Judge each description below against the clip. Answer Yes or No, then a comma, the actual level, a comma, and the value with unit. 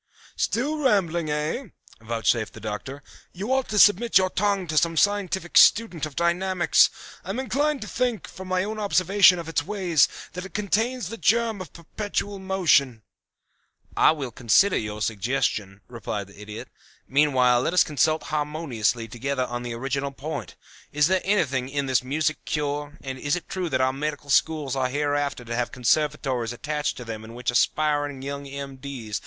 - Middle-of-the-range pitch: Yes, medium, 150 Hz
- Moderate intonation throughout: No, wide, 6.5 semitones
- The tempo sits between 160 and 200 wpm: Yes, average, 170 wpm